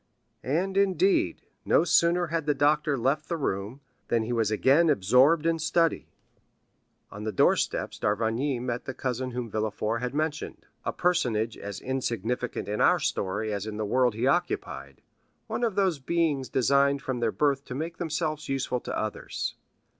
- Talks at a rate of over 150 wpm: Yes, average, 160 wpm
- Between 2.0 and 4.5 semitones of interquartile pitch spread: No, wide, 5.6 semitones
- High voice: No, low, 135 Hz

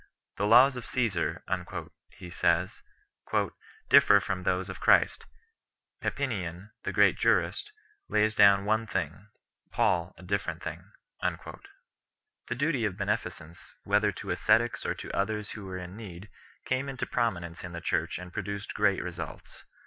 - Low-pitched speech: Yes, low, 100 Hz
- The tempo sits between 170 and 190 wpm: No, average, 145 wpm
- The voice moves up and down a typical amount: Yes, average, 3.4 semitones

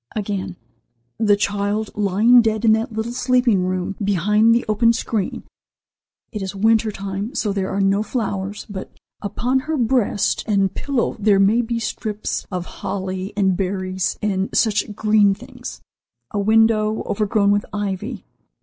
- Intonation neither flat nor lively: No, narrow, 2.2 semitones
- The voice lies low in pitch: No, high, 210 Hz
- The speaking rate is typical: Yes, average, 150 wpm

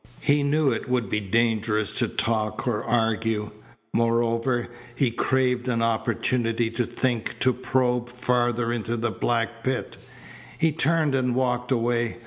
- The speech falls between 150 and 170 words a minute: No, average, 140 wpm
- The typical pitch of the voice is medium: No, low, 120 Hz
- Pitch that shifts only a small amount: Yes, narrow, 1.7 semitones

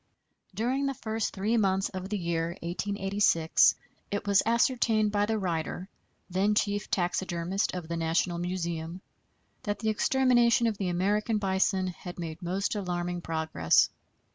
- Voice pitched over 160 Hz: Yes, high, 190 Hz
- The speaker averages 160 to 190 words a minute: No, average, 140 wpm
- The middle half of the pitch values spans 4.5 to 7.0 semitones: No, average, 3.4 semitones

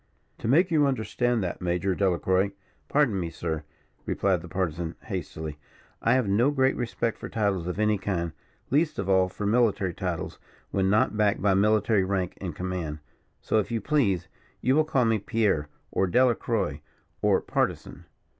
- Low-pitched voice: Yes, low, 100 Hz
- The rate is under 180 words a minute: Yes, average, 170 wpm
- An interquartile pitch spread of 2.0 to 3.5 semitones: No, average, 4.3 semitones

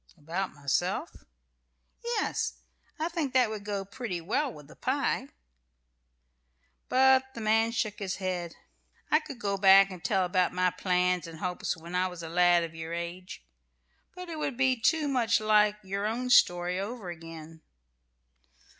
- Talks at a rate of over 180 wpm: No, average, 160 wpm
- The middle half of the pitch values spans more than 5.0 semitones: Yes, wide, 5.5 semitones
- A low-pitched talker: No, high, 195 Hz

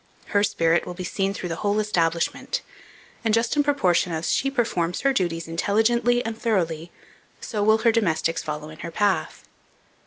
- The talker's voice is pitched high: Yes, high, 195 Hz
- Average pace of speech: Yes, average, 175 wpm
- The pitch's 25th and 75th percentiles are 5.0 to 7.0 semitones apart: Yes, average, 5.3 semitones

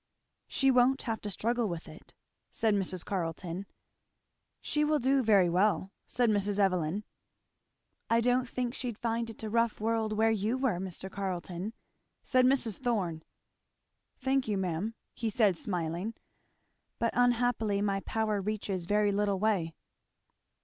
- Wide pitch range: No, average, 3.6 semitones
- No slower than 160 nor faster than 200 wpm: No, average, 145 wpm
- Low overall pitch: No, high, 215 Hz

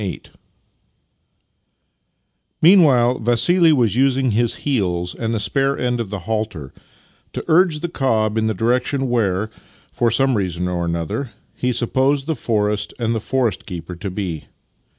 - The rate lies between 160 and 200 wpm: No, average, 150 wpm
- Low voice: Yes, low, 115 Hz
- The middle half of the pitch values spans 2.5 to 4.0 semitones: No, average, 4.6 semitones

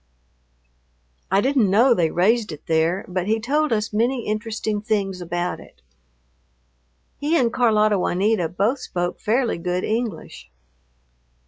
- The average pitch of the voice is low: No, high, 210 Hz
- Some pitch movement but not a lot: Yes, average, 4.5 semitones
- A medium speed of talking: No, slow, 130 wpm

